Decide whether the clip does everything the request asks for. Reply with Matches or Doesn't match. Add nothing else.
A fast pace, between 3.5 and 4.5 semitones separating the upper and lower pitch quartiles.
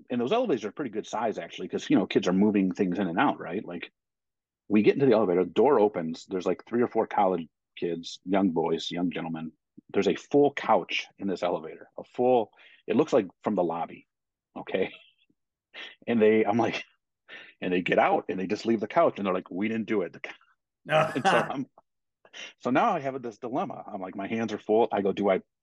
Matches